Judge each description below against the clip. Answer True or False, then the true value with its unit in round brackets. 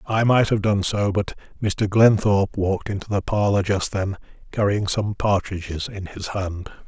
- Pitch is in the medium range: False (100 Hz)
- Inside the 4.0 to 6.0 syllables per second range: True (4.7 syllables/s)